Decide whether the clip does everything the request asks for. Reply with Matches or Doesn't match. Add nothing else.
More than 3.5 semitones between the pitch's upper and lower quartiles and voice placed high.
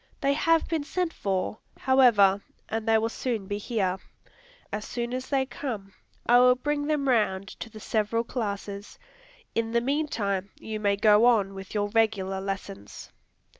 Matches